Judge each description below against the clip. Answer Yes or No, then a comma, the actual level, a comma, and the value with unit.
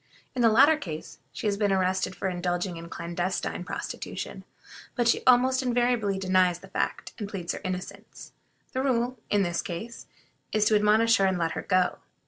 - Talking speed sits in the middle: Yes, average, 180 wpm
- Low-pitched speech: No, high, 195 Hz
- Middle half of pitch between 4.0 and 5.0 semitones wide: Yes, average, 4.5 semitones